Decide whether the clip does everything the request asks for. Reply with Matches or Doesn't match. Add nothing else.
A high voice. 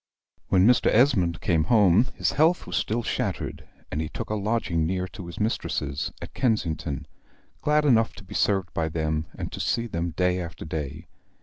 Doesn't match